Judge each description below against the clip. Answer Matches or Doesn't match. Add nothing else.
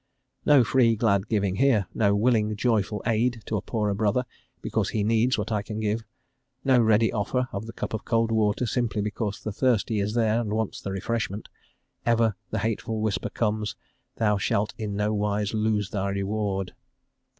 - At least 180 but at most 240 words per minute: Matches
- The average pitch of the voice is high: Doesn't match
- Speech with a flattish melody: Matches